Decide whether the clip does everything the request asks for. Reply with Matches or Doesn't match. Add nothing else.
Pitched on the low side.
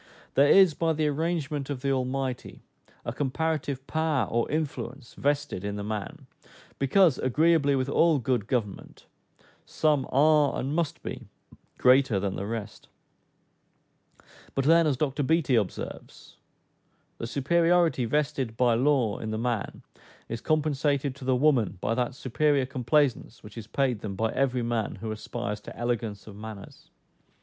Matches